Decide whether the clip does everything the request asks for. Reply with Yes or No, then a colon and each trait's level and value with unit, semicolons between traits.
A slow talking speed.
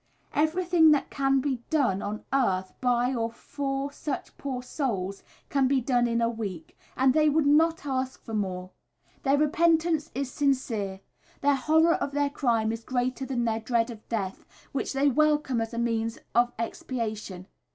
No: average, 170 wpm